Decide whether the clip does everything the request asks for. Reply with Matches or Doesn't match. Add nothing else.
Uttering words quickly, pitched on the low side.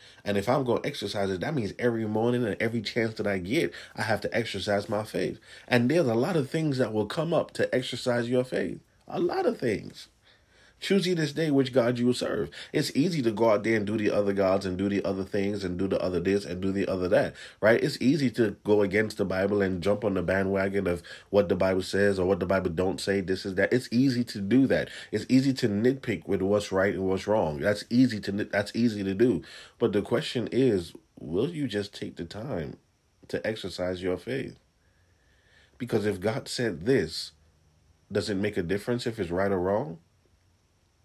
Matches